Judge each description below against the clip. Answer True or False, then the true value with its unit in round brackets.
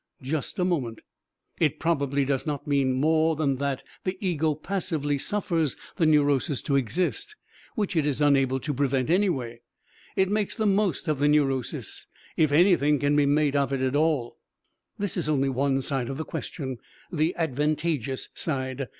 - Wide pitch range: False (3.2 semitones)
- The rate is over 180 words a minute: False (165 wpm)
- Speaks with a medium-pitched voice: True (145 Hz)